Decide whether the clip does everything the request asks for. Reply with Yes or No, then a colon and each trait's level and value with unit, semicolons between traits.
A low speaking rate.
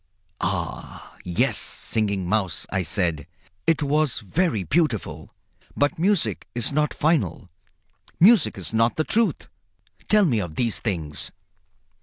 Yes: slow, 125 wpm